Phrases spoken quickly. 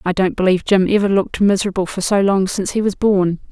Yes: fast, 240 wpm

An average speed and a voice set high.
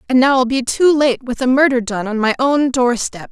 No: fast, 255 wpm; very high, 255 Hz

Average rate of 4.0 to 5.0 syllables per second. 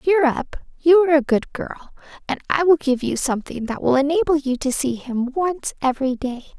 No: 5.4 syllables/s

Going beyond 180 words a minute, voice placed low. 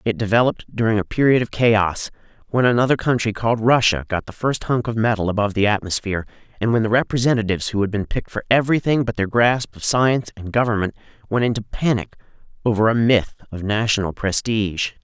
Yes: average, 190 wpm; low, 110 Hz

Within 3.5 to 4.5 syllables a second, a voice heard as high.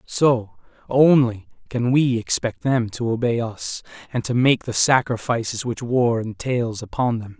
No: 4.2 syllables/s; low, 120 Hz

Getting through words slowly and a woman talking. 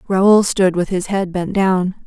No: fast, 205 wpm; female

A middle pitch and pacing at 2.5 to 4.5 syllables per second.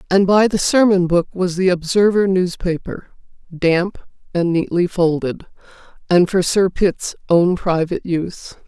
Yes: medium, 180 Hz; 4.4 syllables/s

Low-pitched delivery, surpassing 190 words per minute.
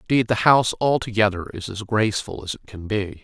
Yes: low, 105 Hz; fast, 205 wpm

